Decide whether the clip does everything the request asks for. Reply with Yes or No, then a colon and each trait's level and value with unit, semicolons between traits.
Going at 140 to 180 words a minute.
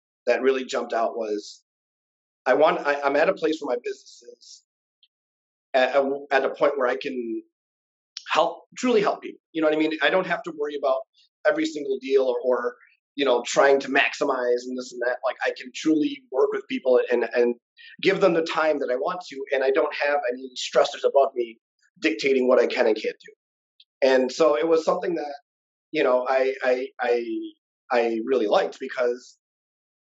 No: average, 200 wpm